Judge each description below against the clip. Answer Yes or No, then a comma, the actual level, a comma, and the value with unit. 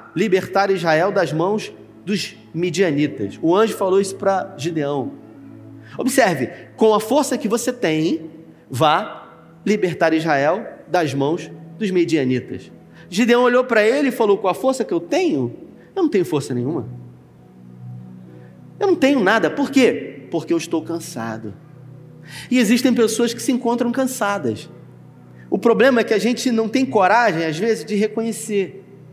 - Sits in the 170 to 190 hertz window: Yes, medium, 185 Hz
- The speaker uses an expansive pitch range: Yes, wide, 8.3 semitones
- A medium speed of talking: Yes, average, 150 wpm